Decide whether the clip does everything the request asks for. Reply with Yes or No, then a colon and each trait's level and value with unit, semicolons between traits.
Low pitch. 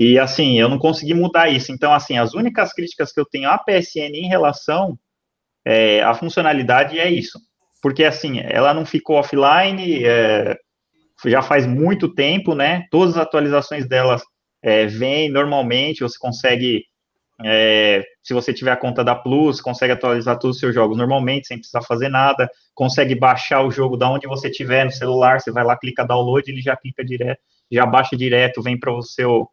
Yes: low, 130 Hz